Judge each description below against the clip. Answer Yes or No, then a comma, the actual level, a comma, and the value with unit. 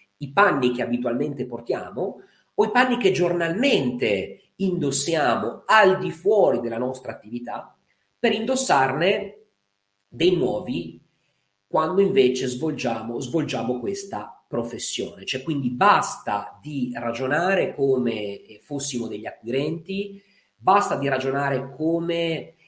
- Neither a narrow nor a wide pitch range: No, wide, 6.9 semitones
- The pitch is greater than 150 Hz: No, medium, 140 Hz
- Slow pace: Yes, slow, 105 wpm